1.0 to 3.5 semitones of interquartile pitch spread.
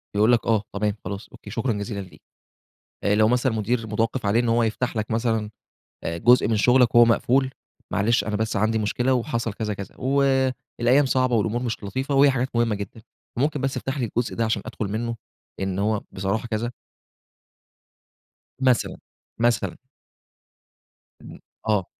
Yes: average, 2.7 semitones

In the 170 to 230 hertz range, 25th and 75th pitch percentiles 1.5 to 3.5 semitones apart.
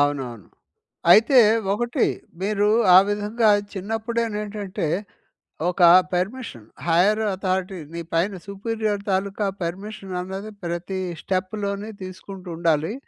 Yes: high, 195 Hz; average, 2.8 semitones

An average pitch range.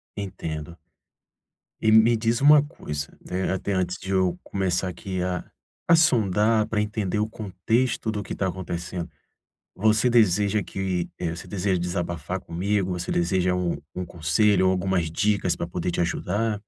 Yes: average, 3.2 semitones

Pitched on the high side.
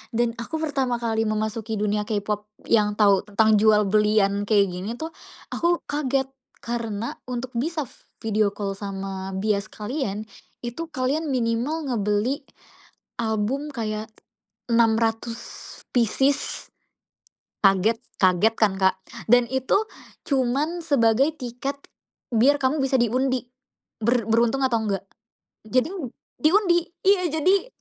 Yes: high, 230 Hz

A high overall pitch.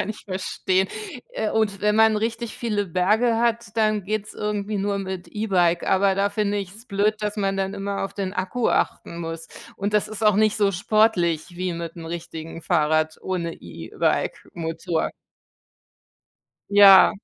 Yes: high, 200 Hz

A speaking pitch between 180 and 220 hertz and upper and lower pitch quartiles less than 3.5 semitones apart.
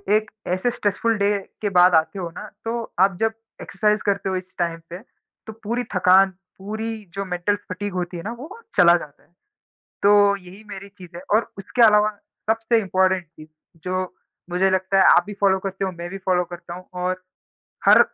Yes: high, 190 Hz; narrow, 2.6 semitones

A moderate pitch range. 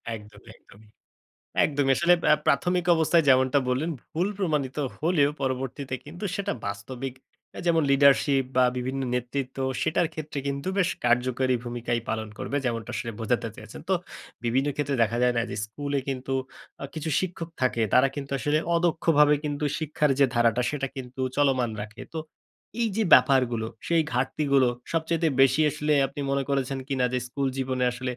Yes: average, 3.2 semitones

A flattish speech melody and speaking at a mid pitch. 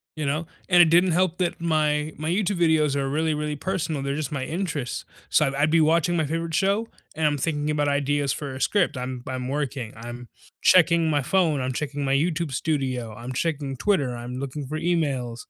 No: average, 3.5 semitones; medium, 150 Hz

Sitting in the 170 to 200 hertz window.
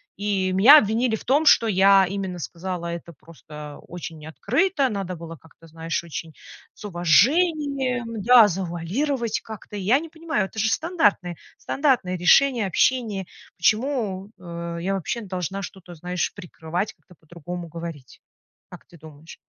Yes: high, 190 Hz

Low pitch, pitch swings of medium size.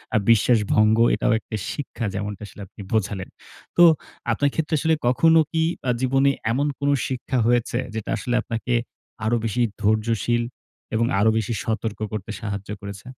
Yes: low, 115 Hz; average, 3.1 semitones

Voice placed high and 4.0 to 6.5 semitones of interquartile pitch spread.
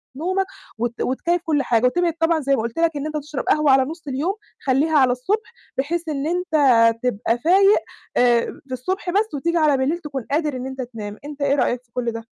Yes: very high, 285 Hz; average, 4.8 semitones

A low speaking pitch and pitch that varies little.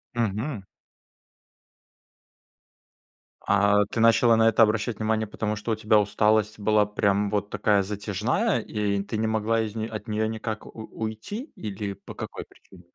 Yes: low, 110 Hz; narrow, 1.4 semitones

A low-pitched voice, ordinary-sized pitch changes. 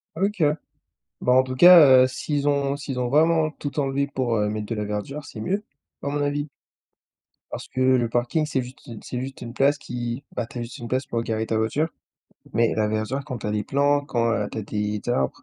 Yes: low, 130 Hz; average, 3.7 semitones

